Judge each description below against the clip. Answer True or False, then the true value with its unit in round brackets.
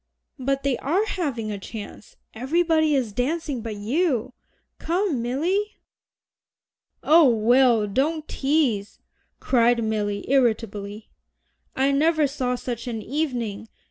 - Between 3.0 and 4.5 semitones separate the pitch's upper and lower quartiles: False (5.5 semitones)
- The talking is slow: True (110 wpm)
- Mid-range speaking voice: False (255 Hz)